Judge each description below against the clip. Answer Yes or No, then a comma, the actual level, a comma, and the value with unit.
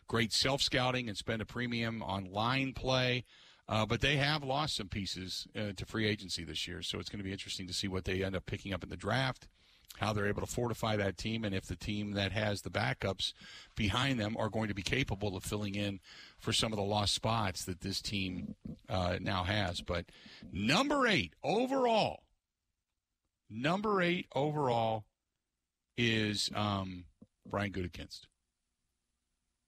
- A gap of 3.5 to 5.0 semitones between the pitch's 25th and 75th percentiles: Yes, average, 3.9 semitones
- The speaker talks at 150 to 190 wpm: Yes, average, 180 wpm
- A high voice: No, low, 105 Hz